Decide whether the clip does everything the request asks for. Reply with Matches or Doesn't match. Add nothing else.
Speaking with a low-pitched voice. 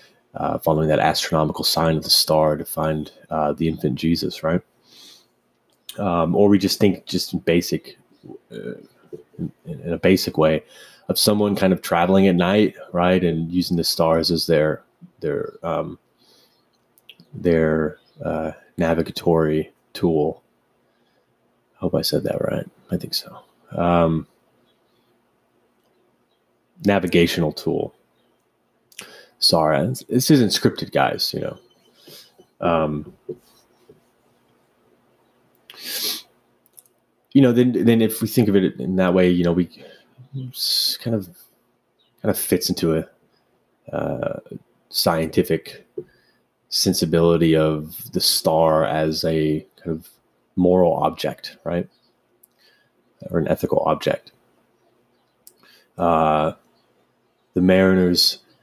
Matches